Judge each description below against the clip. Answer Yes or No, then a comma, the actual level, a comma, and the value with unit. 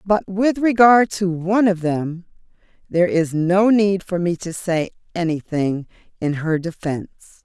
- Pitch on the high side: No, medium, 180 Hz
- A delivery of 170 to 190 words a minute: No, average, 155 wpm